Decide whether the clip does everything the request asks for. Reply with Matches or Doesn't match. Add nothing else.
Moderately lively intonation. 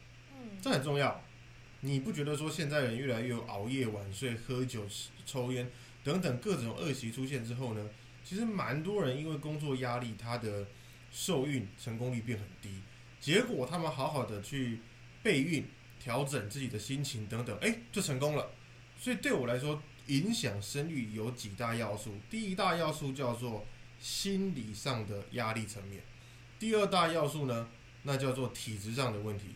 Matches